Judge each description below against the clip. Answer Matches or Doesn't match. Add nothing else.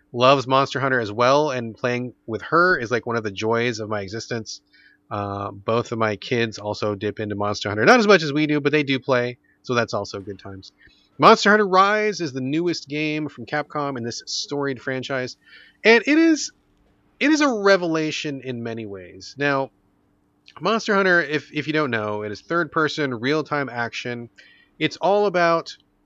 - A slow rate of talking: Doesn't match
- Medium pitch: Doesn't match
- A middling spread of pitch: Doesn't match